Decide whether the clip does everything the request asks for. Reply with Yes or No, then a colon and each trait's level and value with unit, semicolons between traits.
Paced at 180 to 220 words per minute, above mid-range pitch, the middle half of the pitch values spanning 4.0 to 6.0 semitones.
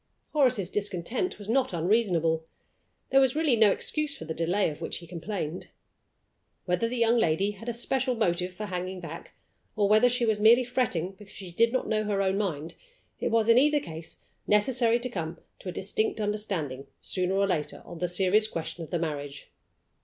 Yes: average, 190 wpm; high, 200 Hz; average, 5.0 semitones